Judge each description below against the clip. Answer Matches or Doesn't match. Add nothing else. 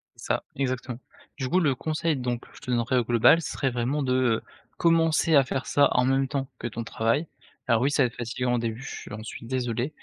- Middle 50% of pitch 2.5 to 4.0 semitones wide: Matches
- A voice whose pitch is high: Doesn't match